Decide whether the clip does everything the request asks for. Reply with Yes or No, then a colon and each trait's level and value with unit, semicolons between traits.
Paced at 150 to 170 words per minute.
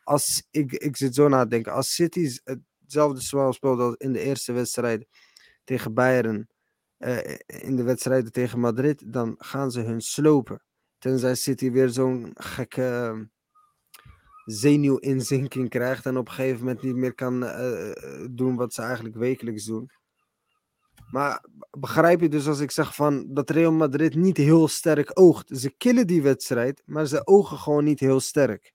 Yes: average, 165 wpm